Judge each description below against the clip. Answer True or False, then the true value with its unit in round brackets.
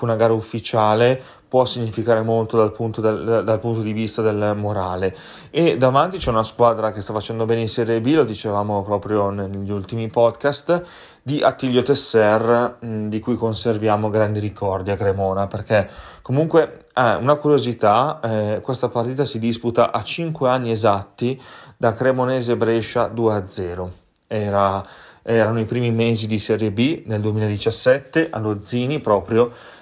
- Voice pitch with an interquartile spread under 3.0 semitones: True (2.4 semitones)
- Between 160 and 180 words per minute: False (150 wpm)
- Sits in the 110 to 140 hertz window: True (115 Hz)